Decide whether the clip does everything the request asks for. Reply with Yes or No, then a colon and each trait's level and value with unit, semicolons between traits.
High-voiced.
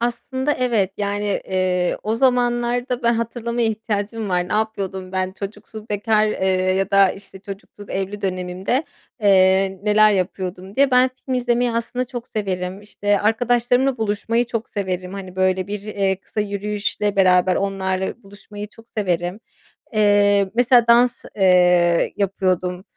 Yes: high, 205 Hz